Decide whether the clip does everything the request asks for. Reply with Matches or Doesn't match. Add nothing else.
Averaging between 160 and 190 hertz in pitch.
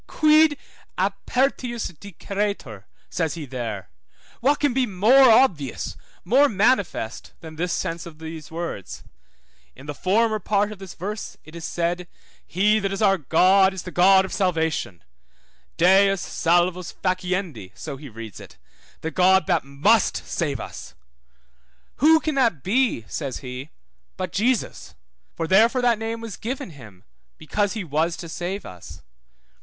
Matches